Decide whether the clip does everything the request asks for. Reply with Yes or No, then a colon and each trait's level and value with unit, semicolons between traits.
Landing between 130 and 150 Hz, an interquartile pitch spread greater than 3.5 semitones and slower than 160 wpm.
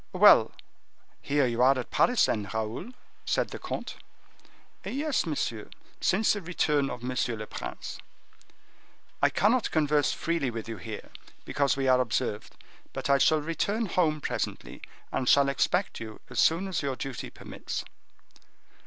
Yes: medium, 140 Hz; wide, 5.5 semitones; average, 150 wpm